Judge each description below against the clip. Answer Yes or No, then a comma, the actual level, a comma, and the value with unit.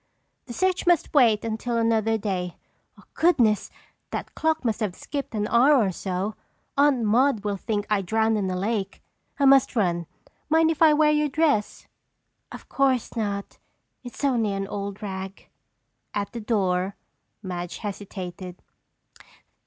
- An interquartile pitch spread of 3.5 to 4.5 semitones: No, average, 5.3 semitones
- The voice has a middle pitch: No, high, 220 Hz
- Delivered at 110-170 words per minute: Yes, average, 145 wpm